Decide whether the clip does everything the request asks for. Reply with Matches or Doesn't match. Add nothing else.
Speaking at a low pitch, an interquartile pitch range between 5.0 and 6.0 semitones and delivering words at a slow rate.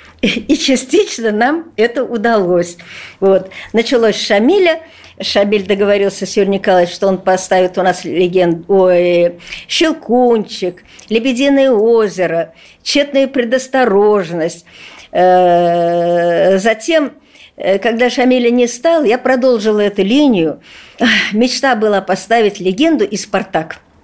Doesn't match